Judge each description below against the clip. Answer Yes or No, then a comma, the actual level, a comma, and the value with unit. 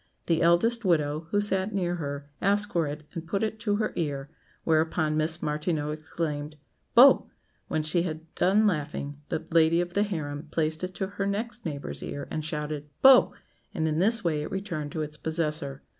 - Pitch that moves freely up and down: No, average, 4.0 semitones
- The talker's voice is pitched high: No, medium, 160 Hz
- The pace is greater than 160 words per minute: Yes, average, 190 wpm